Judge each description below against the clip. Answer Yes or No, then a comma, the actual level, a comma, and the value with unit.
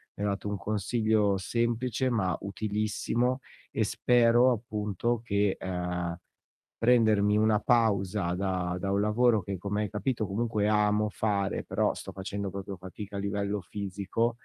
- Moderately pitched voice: No, low, 105 Hz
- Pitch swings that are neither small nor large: No, narrow, 2.3 semitones